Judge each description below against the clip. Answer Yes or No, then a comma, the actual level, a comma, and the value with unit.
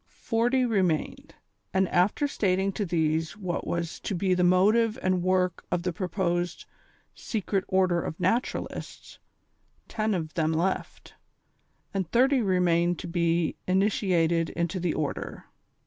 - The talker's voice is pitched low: No, medium, 180 Hz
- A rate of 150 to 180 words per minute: No, slow, 135 wpm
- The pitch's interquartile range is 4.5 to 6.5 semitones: No, narrow, 2.5 semitones